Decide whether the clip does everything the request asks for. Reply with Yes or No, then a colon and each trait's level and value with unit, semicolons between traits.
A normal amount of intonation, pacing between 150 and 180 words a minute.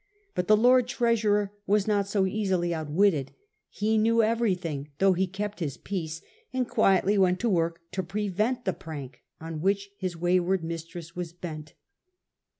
Yes: average, 3.9 semitones; average, 160 wpm